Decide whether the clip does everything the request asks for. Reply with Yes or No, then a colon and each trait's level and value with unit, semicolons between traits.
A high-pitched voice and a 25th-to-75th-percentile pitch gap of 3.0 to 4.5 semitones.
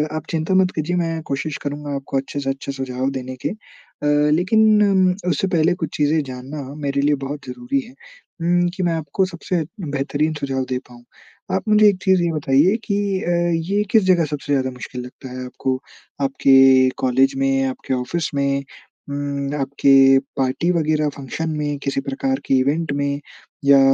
No: medium, 145 Hz; average, 4.2 semitones